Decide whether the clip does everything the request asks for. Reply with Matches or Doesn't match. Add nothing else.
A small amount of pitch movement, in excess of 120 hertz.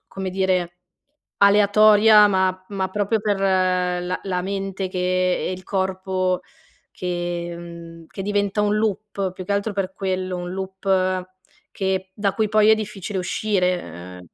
Matches